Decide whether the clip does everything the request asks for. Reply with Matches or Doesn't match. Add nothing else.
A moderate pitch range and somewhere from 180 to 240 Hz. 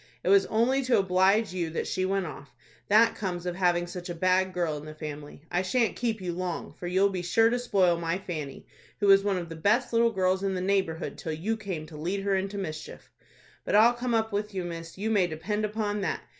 Matches